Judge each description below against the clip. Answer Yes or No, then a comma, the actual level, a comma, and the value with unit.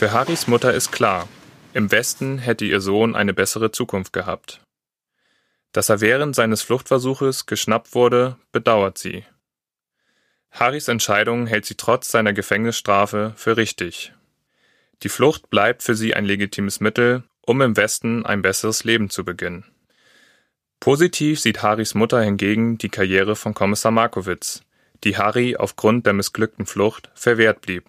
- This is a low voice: Yes, low, 110 Hz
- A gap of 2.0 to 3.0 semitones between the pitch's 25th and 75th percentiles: Yes, narrow, 2.6 semitones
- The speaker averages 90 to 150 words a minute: Yes, average, 140 wpm